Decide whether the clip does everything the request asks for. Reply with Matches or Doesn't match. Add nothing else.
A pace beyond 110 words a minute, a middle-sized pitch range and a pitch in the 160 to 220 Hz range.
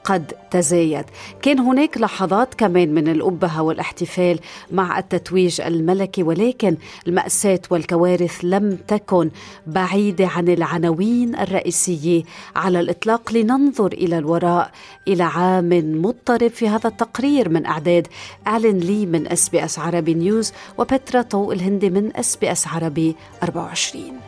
Matches